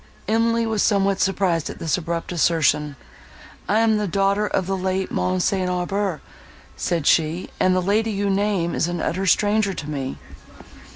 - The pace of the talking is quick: No, average, 170 wpm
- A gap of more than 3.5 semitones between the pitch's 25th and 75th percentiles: No, average, 3.0 semitones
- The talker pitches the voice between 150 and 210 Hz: Yes, high, 190 Hz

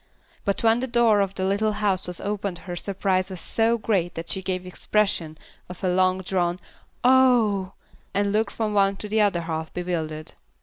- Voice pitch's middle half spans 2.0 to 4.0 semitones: Yes, average, 2.8 semitones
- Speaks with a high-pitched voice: Yes, high, 195 Hz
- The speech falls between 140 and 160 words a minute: No, average, 190 wpm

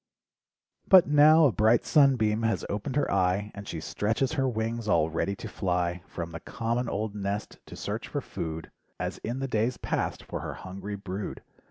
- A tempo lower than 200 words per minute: Yes, average, 185 wpm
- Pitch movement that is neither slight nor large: Yes, average, 4.3 semitones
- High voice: No, low, 105 Hz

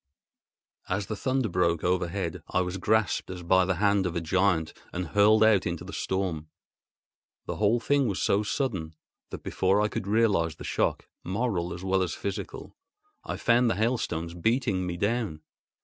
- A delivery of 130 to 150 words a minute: No, average, 175 wpm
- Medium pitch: No, very low, 95 Hz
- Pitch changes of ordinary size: Yes, average, 3.6 semitones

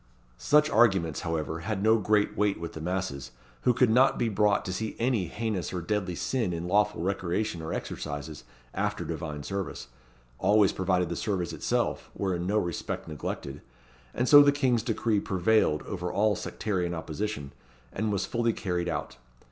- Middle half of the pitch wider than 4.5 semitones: No, average, 4.2 semitones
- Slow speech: No, average, 170 wpm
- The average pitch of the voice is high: No, very low, 95 Hz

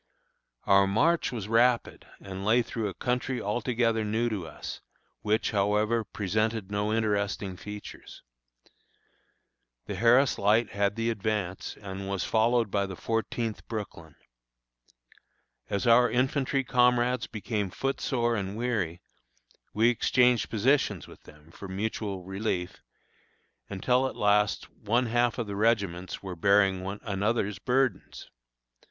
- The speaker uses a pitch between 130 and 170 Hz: No, low, 110 Hz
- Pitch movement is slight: No, average, 3.1 semitones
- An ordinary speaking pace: No, slow, 130 wpm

